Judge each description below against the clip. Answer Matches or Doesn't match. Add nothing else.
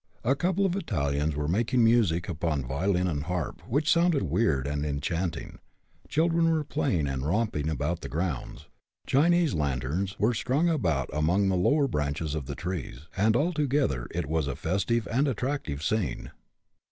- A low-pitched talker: Matches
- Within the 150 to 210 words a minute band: Matches